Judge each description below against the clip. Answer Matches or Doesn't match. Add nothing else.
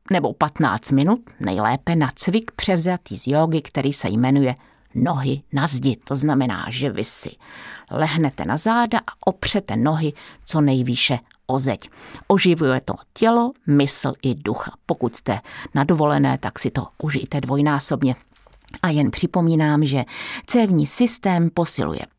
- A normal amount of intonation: Matches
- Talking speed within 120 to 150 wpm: Matches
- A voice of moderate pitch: Matches